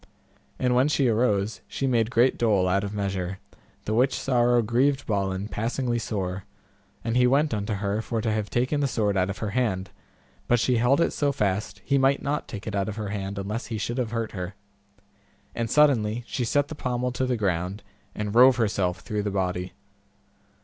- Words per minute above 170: Yes, average, 200 wpm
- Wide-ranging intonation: No, average, 3.9 semitones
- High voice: No, low, 110 Hz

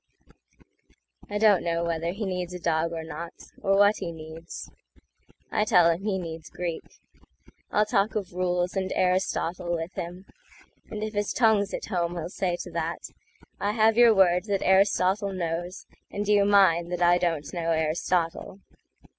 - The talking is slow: No, average, 150 wpm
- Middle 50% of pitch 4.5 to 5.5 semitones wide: No, average, 3.1 semitones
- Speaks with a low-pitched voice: No, medium, 180 Hz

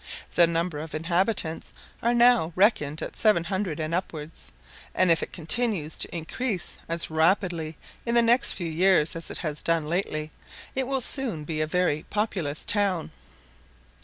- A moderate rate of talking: Yes, average, 160 wpm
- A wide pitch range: No, average, 4.5 semitones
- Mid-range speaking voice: Yes, medium, 170 Hz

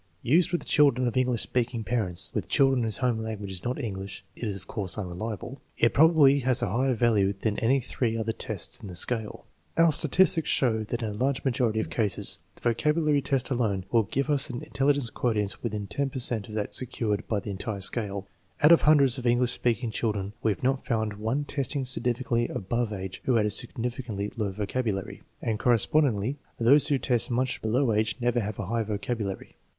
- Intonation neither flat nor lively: Yes, average, 3.7 semitones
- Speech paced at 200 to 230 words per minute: Yes, fast, 205 wpm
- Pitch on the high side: No, low, 115 Hz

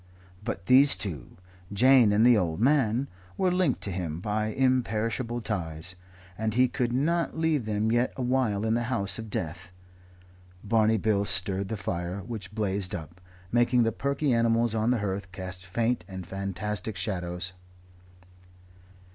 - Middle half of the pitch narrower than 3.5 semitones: No, average, 4.2 semitones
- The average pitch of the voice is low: Yes, low, 110 Hz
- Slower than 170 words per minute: Yes, average, 150 wpm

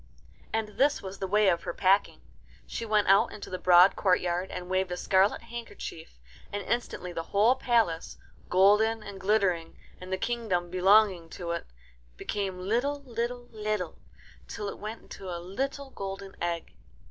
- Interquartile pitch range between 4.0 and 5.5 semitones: No, average, 3.4 semitones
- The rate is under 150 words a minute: No, average, 160 wpm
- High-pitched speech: Yes, high, 195 Hz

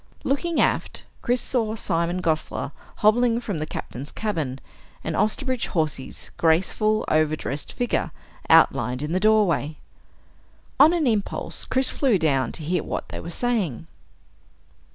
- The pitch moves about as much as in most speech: No, wide, 7.2 semitones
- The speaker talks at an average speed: No, slow, 130 wpm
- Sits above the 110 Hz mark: Yes, medium, 185 Hz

